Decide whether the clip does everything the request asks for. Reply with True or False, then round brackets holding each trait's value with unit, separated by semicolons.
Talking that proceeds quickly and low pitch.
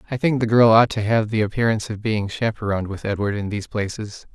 True (235 wpm; 110 Hz)